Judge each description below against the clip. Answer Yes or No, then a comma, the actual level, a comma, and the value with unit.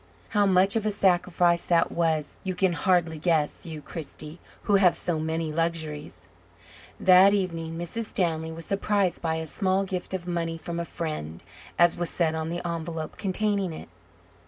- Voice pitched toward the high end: No, medium, 170 Hz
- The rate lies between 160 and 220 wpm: Yes, average, 170 wpm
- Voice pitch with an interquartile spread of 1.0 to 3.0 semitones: Yes, narrow, 2.5 semitones